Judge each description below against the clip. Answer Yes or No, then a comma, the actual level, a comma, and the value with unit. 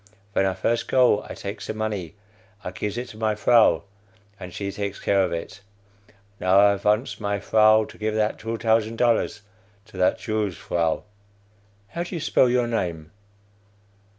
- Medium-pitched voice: No, low, 105 Hz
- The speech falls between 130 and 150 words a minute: No, average, 175 wpm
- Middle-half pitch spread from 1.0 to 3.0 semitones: Yes, narrow, 2.4 semitones